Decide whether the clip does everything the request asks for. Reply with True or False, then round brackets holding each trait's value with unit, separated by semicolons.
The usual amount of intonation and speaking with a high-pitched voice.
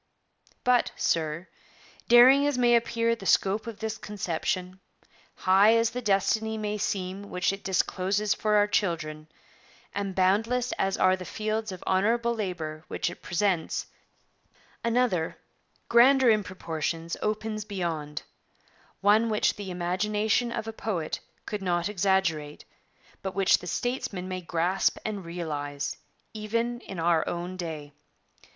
True (3.9 semitones; 195 Hz)